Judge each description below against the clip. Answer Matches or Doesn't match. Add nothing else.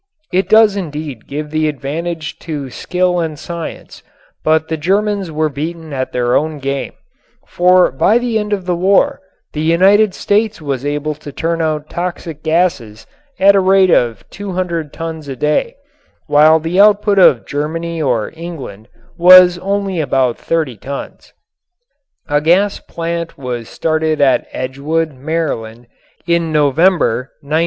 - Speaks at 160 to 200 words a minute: Doesn't match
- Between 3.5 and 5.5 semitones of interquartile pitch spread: Matches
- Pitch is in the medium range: Matches